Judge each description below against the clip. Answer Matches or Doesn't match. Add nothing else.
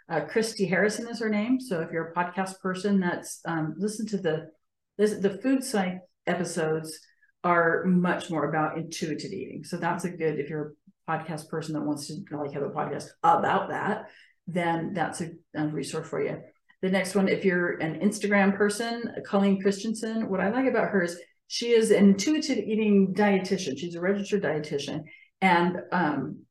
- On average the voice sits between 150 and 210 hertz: Matches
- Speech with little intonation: Doesn't match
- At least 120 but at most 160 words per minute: Doesn't match